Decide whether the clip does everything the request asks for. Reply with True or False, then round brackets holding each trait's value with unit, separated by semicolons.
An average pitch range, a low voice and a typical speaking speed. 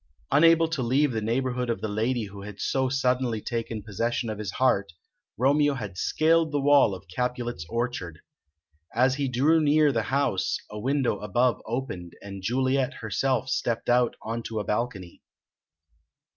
True (3.9 semitones; 120 Hz; 160 wpm)